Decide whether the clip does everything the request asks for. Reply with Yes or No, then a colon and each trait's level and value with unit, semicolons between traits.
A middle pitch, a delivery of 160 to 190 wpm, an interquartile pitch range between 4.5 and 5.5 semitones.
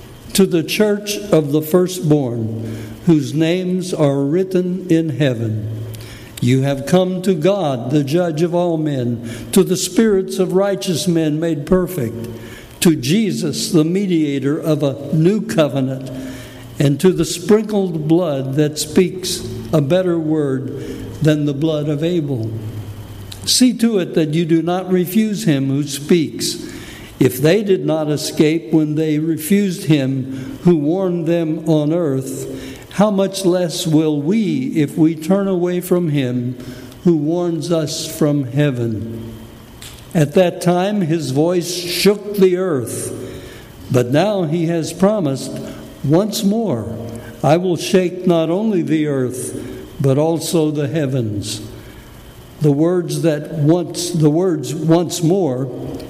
No: medium, 155 Hz; slow, 135 wpm; average, 5.1 semitones